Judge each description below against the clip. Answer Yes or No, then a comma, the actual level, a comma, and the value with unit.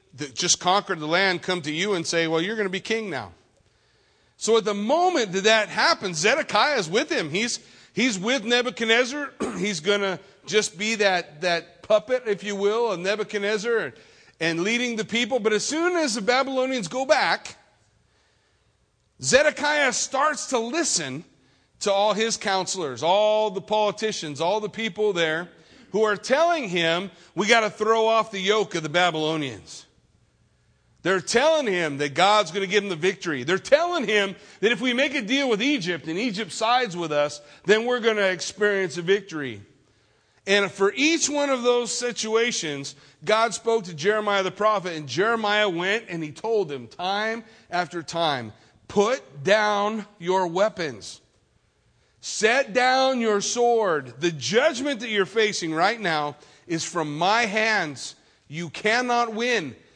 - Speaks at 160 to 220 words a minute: Yes, average, 165 wpm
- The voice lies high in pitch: Yes, high, 205 Hz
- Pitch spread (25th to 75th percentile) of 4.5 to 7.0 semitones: Yes, average, 5.1 semitones